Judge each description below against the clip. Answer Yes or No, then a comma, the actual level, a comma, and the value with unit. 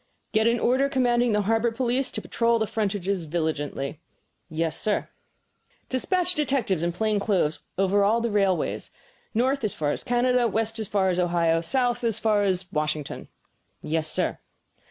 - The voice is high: Yes, high, 210 Hz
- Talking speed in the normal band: Yes, average, 160 wpm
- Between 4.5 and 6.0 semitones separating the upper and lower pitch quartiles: Yes, wide, 5.5 semitones